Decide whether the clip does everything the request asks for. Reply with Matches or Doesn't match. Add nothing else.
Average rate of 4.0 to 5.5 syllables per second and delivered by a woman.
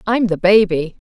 Matches